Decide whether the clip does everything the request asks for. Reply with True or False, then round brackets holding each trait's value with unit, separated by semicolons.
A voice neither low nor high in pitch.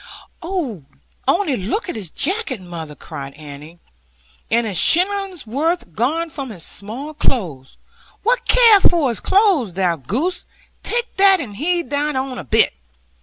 False (270 Hz)